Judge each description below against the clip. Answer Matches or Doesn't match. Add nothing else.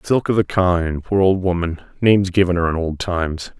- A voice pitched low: Matches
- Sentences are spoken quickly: Matches